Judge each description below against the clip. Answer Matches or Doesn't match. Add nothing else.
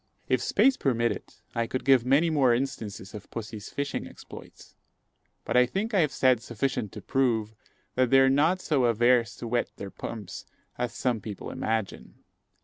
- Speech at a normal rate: Matches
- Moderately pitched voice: Doesn't match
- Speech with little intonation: Doesn't match